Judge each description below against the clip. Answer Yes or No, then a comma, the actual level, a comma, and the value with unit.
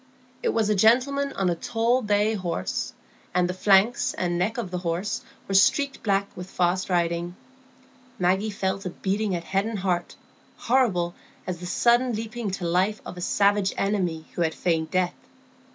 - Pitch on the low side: No, high, 195 Hz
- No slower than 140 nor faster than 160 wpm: No, average, 175 wpm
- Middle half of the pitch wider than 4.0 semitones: No, average, 3.4 semitones